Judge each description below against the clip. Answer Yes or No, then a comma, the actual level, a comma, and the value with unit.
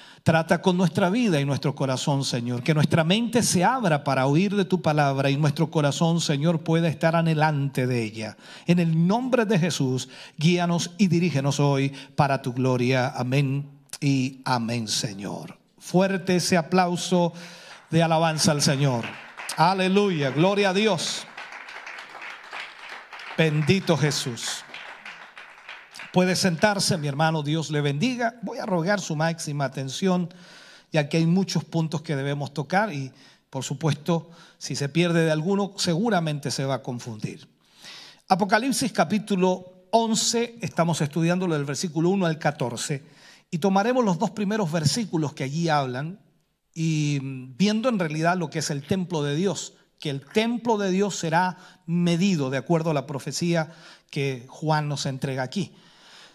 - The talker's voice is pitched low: No, medium, 165 Hz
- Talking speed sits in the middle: Yes, average, 145 wpm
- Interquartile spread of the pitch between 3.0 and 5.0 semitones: Yes, average, 4.6 semitones